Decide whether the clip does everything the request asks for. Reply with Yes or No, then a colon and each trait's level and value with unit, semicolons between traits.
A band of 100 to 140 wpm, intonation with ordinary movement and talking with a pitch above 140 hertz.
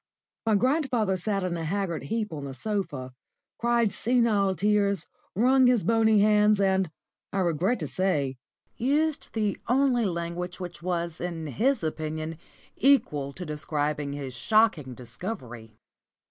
No: slow, 135 wpm; wide, 6.0 semitones; high, 190 Hz